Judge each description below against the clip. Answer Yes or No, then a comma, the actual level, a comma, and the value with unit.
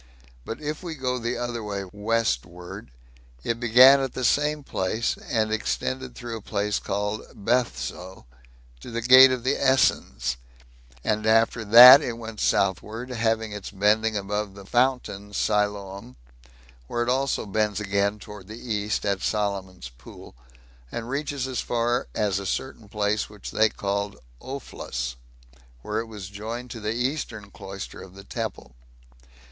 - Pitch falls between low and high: No, low, 110 Hz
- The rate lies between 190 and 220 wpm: No, average, 150 wpm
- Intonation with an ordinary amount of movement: Yes, average, 3.2 semitones